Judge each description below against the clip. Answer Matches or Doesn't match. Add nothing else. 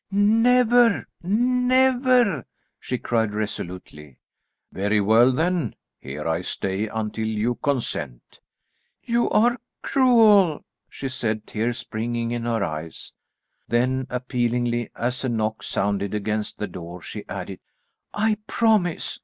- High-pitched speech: Doesn't match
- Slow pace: Matches